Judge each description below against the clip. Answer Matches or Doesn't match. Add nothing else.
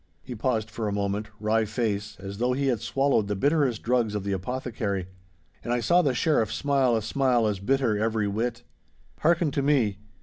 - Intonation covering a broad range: Doesn't match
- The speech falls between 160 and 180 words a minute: Doesn't match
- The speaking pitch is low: Matches